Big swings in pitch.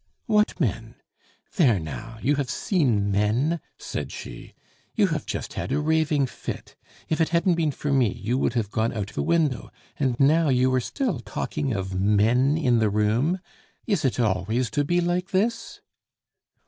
Yes: wide, 6.5 semitones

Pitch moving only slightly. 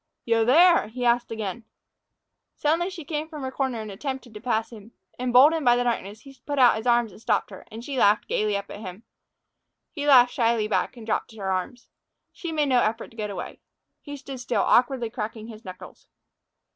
No: average, 3.7 semitones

